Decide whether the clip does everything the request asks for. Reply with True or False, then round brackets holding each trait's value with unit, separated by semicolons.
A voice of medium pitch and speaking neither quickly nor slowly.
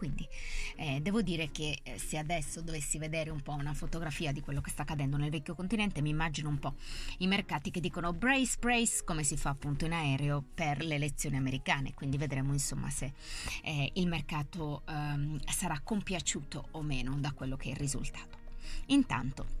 False (150 Hz; 185 wpm)